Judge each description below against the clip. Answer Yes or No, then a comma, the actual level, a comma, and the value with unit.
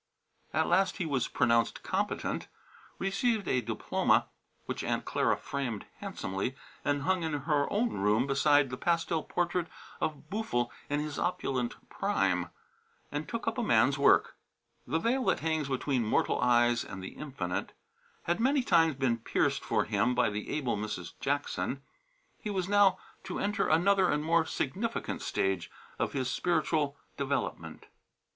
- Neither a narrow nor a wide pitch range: No, wide, 6.1 semitones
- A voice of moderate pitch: Yes, medium, 145 Hz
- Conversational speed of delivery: Yes, average, 150 wpm